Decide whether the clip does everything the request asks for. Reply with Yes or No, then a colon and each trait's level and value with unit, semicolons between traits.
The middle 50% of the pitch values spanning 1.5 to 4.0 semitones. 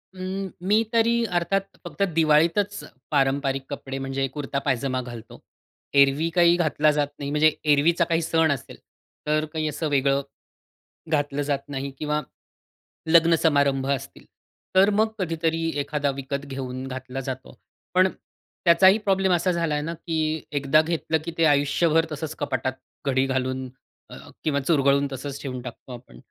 Yes: average, 3.4 semitones